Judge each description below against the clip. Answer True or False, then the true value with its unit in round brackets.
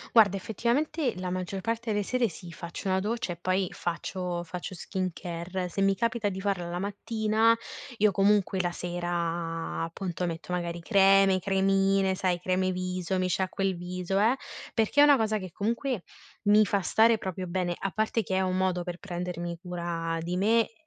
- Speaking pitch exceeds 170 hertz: True (190 Hz)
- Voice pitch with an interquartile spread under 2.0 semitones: False (2.7 semitones)